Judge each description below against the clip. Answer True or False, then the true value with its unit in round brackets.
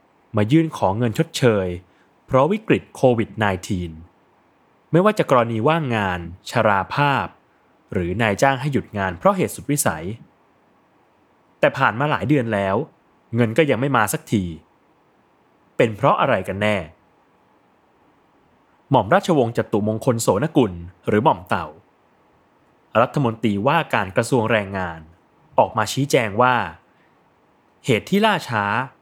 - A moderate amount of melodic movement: False (6.2 semitones)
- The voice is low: True (110 Hz)